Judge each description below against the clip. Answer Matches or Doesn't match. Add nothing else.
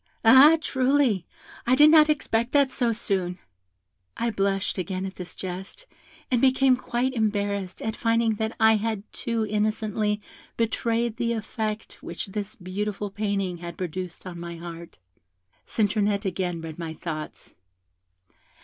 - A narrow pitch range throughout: Doesn't match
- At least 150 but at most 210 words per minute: Doesn't match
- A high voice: Matches